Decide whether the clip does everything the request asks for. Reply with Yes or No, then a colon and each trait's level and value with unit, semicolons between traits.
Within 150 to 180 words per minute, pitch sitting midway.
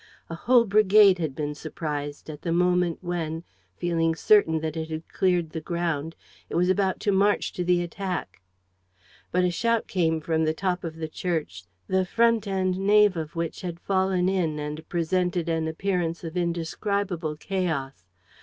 Yes: average, 170 wpm; medium, 175 Hz